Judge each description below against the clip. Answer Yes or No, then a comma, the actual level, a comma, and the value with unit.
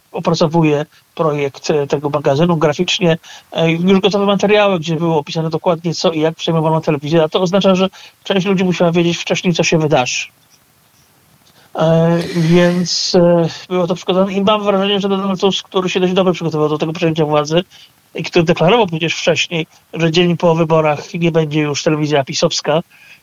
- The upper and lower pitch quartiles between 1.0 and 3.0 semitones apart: Yes, narrow, 2.6 semitones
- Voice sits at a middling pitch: Yes, medium, 170 Hz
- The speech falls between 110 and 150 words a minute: No, fast, 160 wpm